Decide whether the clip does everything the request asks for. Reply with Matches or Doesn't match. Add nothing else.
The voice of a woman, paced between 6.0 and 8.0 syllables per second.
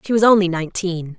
Matches